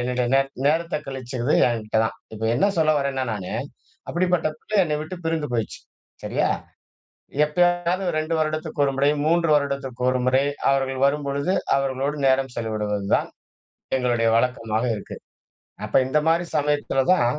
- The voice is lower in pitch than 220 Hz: Yes, low, 135 Hz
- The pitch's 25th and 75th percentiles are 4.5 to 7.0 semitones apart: No, average, 3.9 semitones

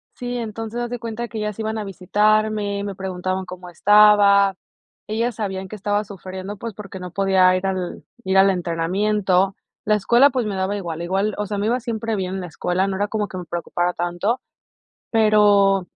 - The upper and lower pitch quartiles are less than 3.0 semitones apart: Yes, narrow, 2.4 semitones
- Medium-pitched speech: No, high, 200 Hz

